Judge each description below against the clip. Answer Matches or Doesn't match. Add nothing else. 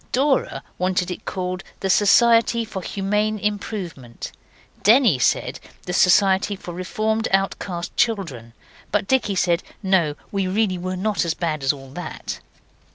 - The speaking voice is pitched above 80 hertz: Matches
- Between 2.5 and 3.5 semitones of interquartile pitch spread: Matches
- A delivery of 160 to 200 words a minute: Doesn't match